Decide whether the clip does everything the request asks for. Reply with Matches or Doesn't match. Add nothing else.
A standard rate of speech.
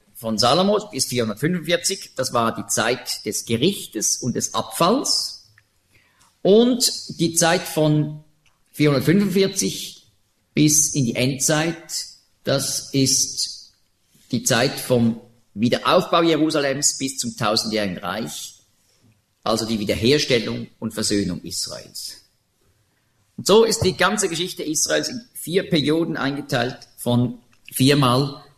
Doesn't match